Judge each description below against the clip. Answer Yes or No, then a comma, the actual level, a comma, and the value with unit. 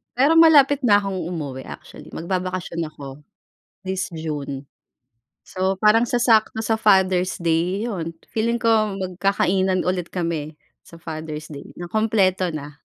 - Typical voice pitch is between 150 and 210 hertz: Yes, medium, 185 Hz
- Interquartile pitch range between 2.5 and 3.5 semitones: No, average, 4.5 semitones